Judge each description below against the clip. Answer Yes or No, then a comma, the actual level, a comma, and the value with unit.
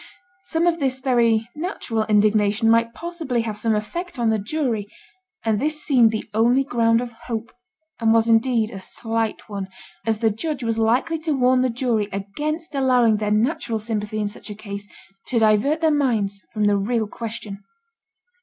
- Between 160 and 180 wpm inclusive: Yes, average, 175 wpm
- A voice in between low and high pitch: No, high, 230 Hz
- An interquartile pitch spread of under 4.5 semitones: Yes, average, 3.4 semitones